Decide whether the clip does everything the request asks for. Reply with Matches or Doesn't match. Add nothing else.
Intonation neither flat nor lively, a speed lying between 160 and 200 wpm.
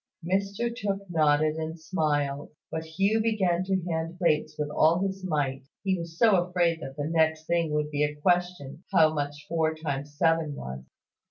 Matches